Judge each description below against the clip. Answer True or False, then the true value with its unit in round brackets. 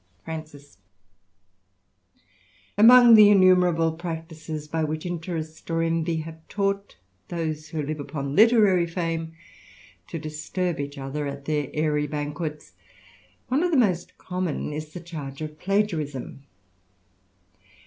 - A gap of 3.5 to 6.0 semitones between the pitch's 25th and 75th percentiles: False (3.0 semitones)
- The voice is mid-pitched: True (160 Hz)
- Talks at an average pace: False (130 wpm)